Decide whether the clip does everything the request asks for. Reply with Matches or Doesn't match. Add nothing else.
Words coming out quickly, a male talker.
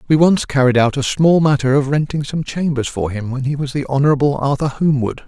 Matches